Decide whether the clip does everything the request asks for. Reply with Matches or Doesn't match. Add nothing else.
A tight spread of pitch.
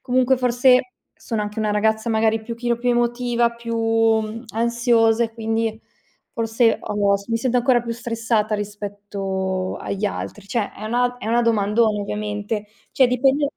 Matches